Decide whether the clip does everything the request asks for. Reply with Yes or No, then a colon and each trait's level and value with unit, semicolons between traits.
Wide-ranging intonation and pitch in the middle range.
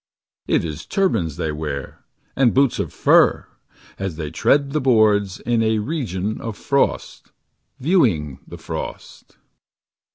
No: wide, 8.6 semitones; low, 110 Hz